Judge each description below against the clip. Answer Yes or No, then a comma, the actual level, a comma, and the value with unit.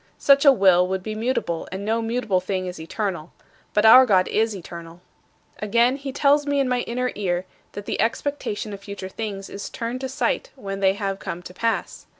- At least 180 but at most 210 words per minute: Yes, average, 200 wpm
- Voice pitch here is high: Yes, high, 210 Hz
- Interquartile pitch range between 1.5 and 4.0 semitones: No, average, 4.8 semitones